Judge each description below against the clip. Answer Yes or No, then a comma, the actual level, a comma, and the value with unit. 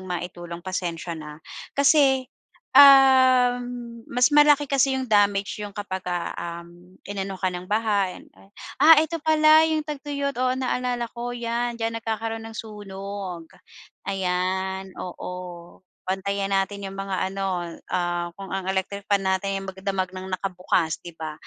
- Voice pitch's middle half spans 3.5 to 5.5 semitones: Yes, average, 5.0 semitones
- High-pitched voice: Yes, high, 195 Hz